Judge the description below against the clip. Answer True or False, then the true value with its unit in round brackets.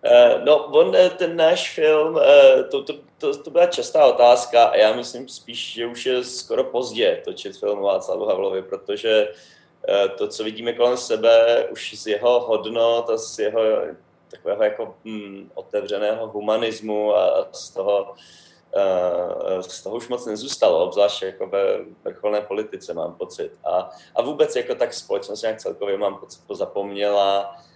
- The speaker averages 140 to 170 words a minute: True (150 wpm)